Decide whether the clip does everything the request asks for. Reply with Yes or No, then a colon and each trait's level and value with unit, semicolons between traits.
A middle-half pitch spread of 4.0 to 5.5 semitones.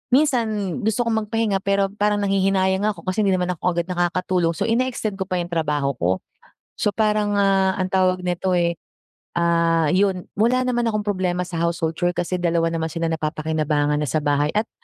No: average, 3.5 semitones